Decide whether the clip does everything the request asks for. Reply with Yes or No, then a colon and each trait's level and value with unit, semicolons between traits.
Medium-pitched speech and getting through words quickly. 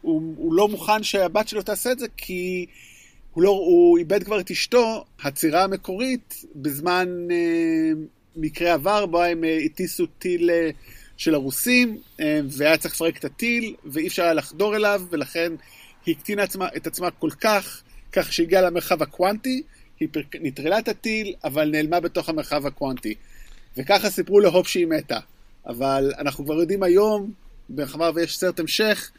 Yes: medium, 180 Hz; fast, 160 wpm